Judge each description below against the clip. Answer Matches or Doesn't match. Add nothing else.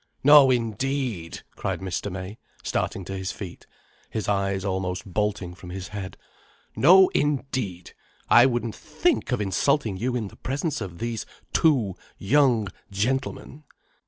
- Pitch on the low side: Matches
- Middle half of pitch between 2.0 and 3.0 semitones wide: Doesn't match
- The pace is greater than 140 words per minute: Doesn't match